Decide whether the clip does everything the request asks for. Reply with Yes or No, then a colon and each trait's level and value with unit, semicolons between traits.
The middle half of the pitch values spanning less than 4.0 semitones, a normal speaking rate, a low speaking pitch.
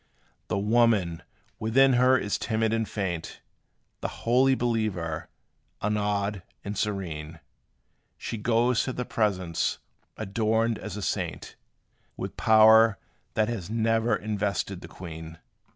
No: narrow, 2.6 semitones; slow, 120 wpm; low, 110 Hz